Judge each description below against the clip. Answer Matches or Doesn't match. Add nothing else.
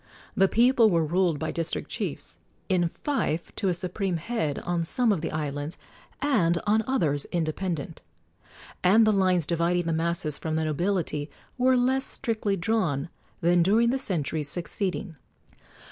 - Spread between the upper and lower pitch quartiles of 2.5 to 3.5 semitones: Doesn't match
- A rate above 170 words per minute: Doesn't match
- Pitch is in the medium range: Matches